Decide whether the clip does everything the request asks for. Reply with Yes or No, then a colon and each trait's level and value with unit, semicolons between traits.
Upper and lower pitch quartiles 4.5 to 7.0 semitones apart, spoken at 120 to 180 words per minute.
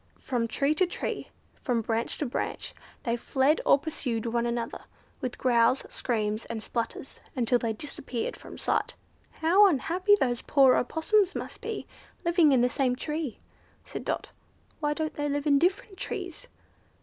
Yes: average, 5.1 semitones; average, 160 wpm